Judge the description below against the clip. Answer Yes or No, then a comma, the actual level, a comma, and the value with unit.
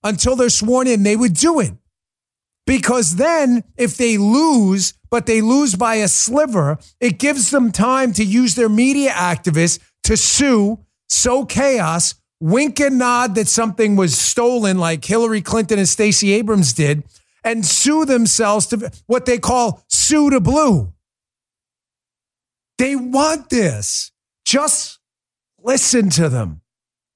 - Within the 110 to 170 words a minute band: Yes, average, 140 wpm